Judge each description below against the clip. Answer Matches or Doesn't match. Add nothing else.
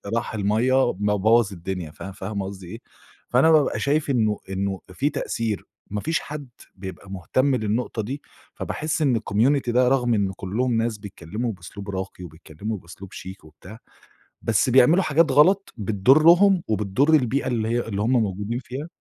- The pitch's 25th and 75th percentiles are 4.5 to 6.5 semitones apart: Matches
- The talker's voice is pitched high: Doesn't match